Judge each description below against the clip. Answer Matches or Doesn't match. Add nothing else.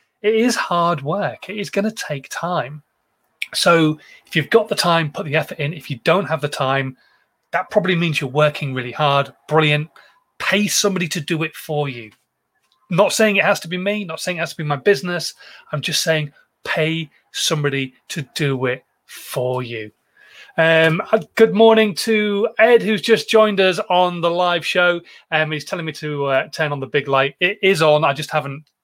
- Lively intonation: Doesn't match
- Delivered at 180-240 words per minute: Matches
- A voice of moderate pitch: Matches